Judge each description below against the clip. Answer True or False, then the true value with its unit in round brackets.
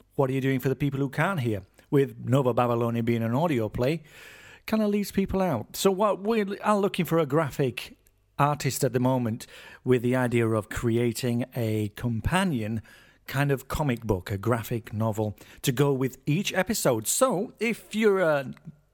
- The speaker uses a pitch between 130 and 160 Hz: True (135 Hz)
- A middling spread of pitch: False (6.2 semitones)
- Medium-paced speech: True (180 wpm)